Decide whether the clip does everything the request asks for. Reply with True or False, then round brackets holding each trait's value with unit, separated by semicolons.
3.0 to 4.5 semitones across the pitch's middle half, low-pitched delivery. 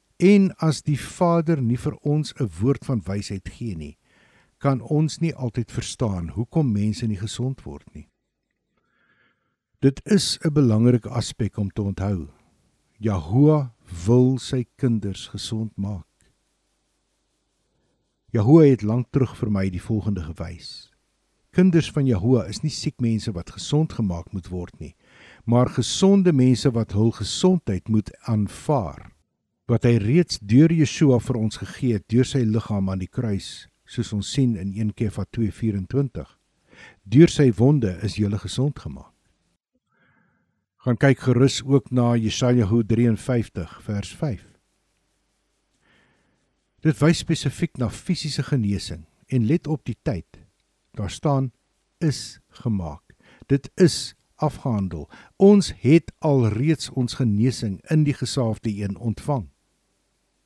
False (5.2 semitones; 120 Hz)